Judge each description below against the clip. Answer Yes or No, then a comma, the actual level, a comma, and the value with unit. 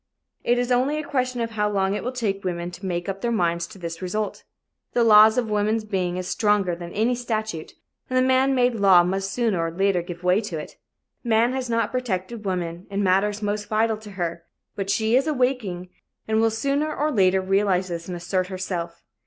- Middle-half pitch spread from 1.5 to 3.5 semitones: No, average, 4.3 semitones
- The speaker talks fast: Yes, fast, 210 wpm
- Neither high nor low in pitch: No, high, 205 Hz